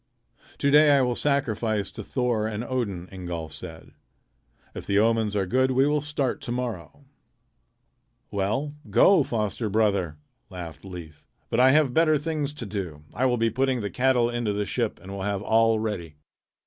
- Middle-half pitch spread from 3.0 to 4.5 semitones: No, average, 5.0 semitones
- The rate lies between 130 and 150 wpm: No, average, 175 wpm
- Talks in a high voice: No, low, 115 Hz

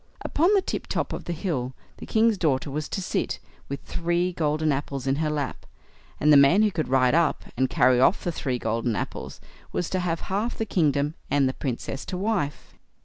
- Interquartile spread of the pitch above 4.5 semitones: Yes, average, 5.0 semitones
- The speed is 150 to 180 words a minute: No, fast, 205 wpm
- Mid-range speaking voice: Yes, medium, 150 Hz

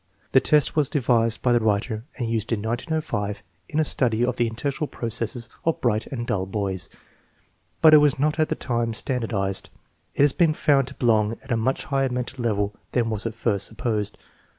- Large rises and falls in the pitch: No, average, 3.7 semitones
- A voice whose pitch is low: Yes, low, 120 Hz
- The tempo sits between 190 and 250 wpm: Yes, average, 195 wpm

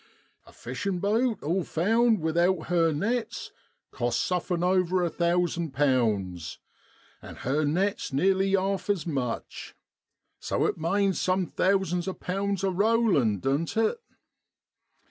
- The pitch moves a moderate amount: Yes, average, 3.9 semitones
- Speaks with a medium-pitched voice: Yes, medium, 180 Hz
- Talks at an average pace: No, slow, 125 wpm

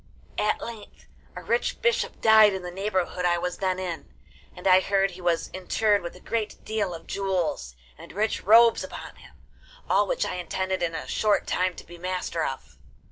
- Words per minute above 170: Yes, average, 190 wpm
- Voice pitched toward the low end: No, medium, 185 Hz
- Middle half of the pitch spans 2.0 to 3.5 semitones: Yes, average, 3.0 semitones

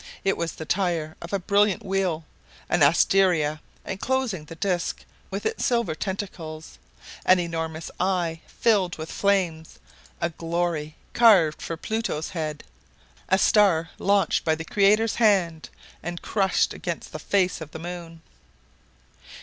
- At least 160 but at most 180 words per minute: No, slow, 135 wpm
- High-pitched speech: No, medium, 175 Hz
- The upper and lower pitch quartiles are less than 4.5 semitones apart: Yes, average, 3.5 semitones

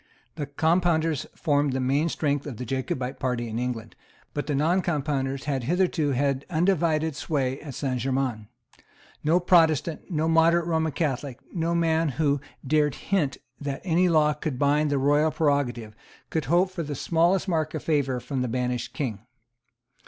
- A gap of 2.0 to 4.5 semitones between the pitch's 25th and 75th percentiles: Yes, average, 3.4 semitones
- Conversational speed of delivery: Yes, average, 165 wpm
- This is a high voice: No, medium, 150 Hz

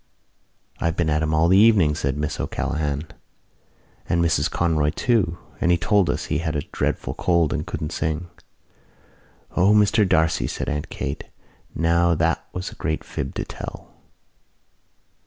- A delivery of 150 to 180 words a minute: Yes, average, 160 wpm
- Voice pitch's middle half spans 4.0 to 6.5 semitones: No, narrow, 2.4 semitones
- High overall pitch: No, very low, 80 Hz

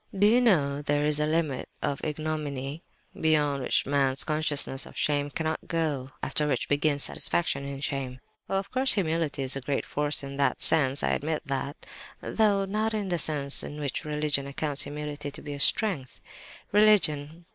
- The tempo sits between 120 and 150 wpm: No, average, 175 wpm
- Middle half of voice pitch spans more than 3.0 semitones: No, narrow, 2.5 semitones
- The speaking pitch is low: No, medium, 150 Hz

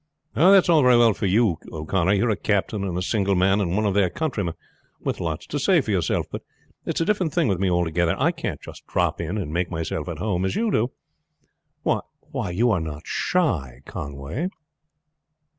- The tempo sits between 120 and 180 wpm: No, fast, 205 wpm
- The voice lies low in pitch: Yes, low, 100 Hz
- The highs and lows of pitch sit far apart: Yes, wide, 5.7 semitones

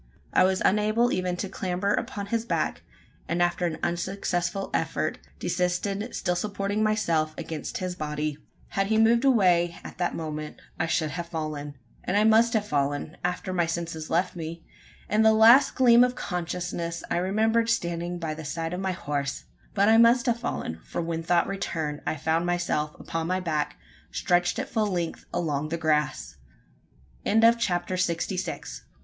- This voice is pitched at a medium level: Yes, medium, 175 Hz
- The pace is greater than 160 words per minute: Yes, average, 170 wpm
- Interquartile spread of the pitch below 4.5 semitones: Yes, average, 3.9 semitones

